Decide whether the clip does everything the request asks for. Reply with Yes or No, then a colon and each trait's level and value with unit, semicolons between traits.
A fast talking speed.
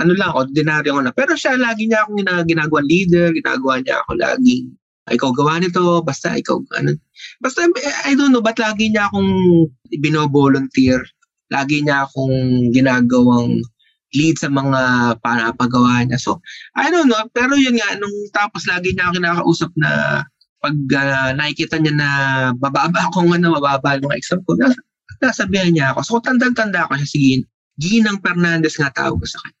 Yes: fast, 170 wpm